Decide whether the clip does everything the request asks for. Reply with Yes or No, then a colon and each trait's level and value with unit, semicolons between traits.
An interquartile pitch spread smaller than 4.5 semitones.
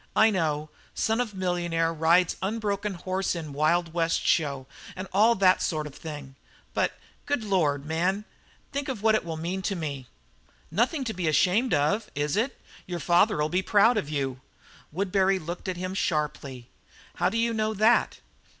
No: average, 5.0 semitones